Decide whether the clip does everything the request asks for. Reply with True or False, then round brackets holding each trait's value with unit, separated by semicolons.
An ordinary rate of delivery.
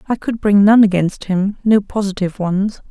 True (165 wpm)